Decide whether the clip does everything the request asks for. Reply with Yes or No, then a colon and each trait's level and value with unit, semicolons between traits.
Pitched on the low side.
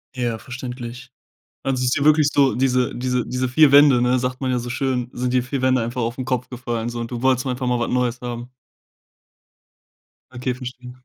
Yes: low, 125 Hz